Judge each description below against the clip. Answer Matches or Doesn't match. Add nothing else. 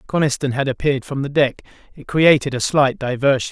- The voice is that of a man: Matches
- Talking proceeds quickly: Doesn't match